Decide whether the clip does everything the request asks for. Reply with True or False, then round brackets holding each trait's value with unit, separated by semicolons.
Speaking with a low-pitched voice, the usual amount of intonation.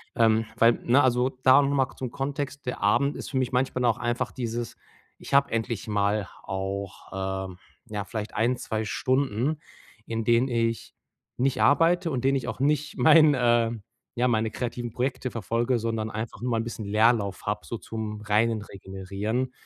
True (120 Hz; 3.1 semitones)